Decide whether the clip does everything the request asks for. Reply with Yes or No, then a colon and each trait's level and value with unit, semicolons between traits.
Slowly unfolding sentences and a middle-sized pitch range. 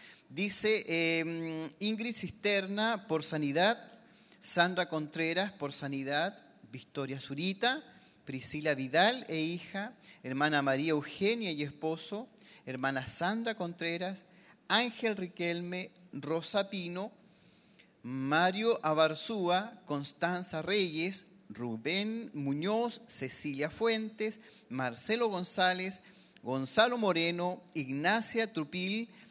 No: slow, 85 wpm; wide, 5.7 semitones